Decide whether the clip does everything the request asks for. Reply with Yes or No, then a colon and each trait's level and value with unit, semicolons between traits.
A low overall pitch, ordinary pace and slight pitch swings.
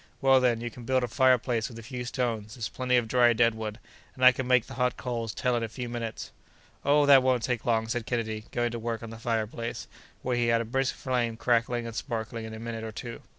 No: low, 120 Hz; fast, 250 wpm; narrow, 1.8 semitones